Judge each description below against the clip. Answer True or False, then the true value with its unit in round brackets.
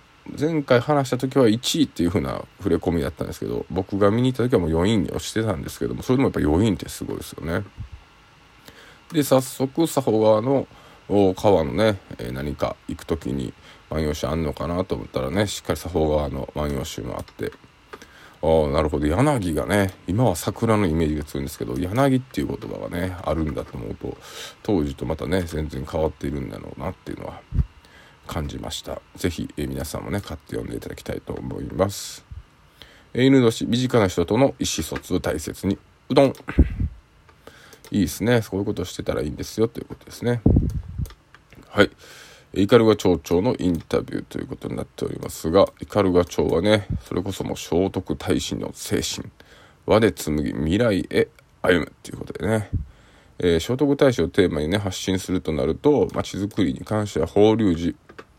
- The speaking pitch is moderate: False (95 Hz)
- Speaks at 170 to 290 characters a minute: False (365 characters per minute)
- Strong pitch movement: True (6.0 semitones)